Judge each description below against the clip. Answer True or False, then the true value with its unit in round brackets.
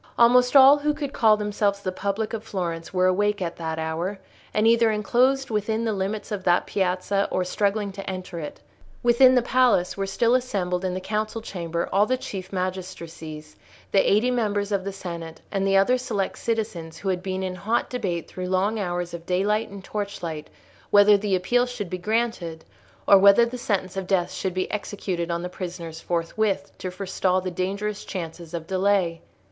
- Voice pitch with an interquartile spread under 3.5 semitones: True (3.1 semitones)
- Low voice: False (195 Hz)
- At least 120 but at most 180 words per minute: False (190 wpm)